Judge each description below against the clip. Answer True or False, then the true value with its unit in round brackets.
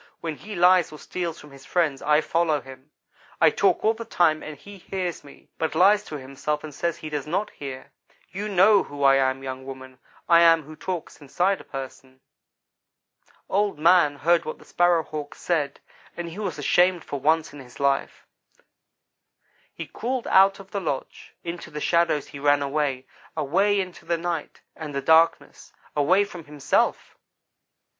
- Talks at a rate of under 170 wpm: False (180 wpm)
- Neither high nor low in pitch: True (160 Hz)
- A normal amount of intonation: True (4.0 semitones)